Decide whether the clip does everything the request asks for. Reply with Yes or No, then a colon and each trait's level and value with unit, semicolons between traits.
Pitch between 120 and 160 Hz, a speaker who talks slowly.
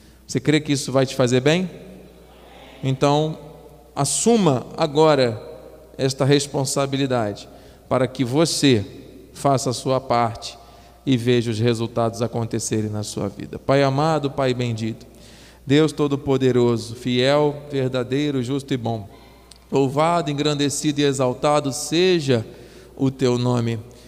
Yes: low, 135 Hz; slow, 115 wpm